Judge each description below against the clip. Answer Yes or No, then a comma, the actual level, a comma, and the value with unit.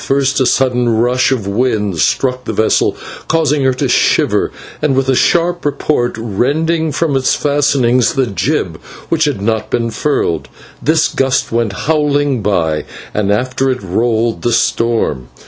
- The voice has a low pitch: Yes, low, 125 Hz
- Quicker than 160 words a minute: No, average, 155 wpm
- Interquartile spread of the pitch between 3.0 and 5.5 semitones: Yes, average, 4.2 semitones